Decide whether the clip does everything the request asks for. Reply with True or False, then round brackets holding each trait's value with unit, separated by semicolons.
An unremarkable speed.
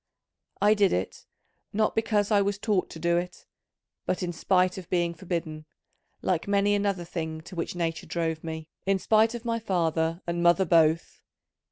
True (175 wpm)